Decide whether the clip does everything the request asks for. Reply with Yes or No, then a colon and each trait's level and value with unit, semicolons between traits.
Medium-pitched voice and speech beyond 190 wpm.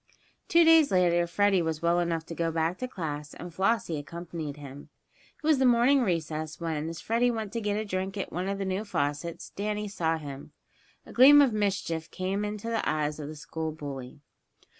Yes: medium, 175 Hz; fast, 205 wpm